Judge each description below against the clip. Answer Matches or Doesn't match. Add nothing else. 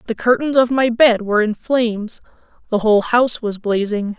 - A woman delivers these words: Matches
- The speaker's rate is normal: Matches